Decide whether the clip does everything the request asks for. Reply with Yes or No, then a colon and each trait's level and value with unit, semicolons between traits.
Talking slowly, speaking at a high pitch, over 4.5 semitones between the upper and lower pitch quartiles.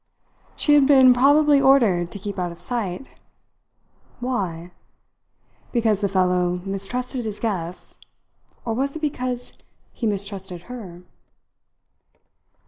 Yes: slow, 115 wpm; high, 215 Hz; wide, 5.6 semitones